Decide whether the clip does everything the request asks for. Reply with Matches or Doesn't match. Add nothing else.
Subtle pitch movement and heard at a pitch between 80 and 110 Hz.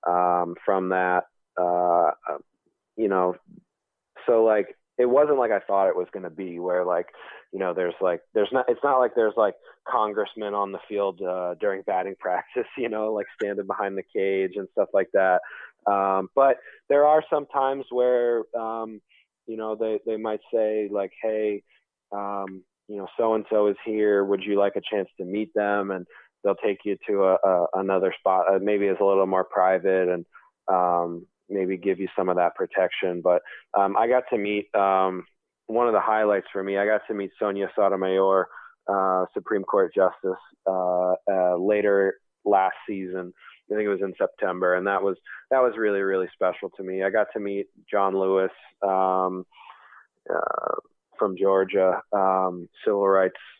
Matches